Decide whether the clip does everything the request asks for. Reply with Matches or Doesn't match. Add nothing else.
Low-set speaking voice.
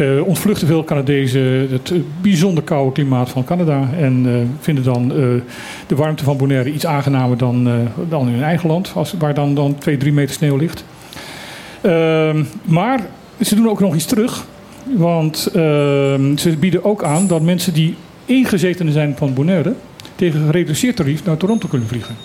Doesn't match